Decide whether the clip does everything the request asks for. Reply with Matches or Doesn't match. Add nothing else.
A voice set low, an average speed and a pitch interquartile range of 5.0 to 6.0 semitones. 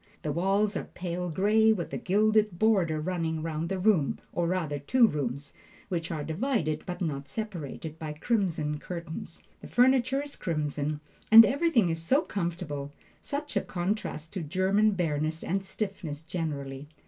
Doesn't match